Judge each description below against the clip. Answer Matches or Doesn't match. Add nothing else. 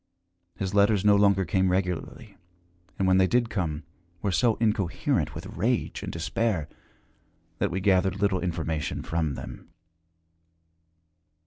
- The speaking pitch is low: Matches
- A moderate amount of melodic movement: Doesn't match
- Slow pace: Matches